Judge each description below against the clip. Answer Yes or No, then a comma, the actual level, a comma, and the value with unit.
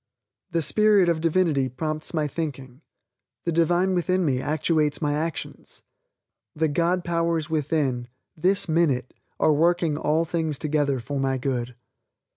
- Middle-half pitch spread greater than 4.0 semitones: No, average, 2.9 semitones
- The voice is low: No, medium, 155 Hz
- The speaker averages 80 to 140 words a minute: Yes, slow, 135 wpm